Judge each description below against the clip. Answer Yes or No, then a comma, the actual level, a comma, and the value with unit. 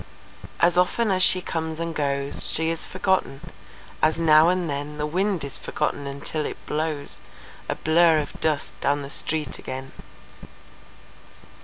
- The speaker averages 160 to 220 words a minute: No, average, 150 wpm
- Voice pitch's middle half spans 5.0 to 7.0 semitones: No, average, 3.0 semitones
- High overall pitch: No, medium, 155 Hz